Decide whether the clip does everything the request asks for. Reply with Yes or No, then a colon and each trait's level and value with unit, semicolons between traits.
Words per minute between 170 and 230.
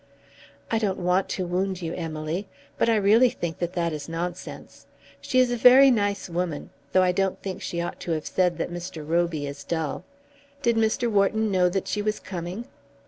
Yes: average, 195 wpm